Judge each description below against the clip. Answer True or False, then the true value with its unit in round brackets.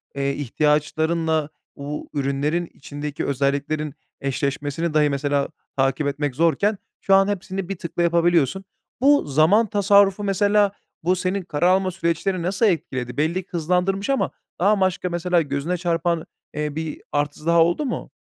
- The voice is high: False (165 Hz)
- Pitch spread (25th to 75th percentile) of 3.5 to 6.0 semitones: True (4.3 semitones)